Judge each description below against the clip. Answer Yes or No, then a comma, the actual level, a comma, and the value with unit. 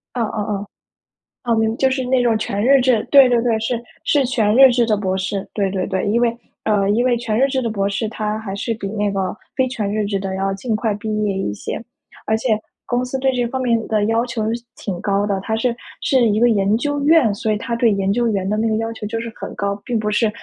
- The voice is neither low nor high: No, high, 220 Hz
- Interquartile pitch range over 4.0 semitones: No, average, 3.0 semitones